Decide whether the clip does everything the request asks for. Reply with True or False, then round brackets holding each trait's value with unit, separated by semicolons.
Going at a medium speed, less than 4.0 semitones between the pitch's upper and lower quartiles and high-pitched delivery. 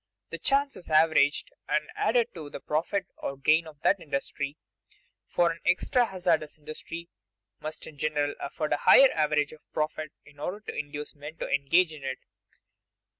False (170 wpm; 2.4 semitones; 155 Hz)